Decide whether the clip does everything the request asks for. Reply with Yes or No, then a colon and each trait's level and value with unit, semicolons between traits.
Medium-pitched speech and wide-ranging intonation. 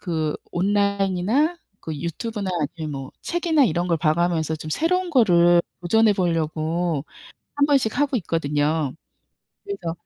Yes: medium, 175 Hz; wide, 6.1 semitones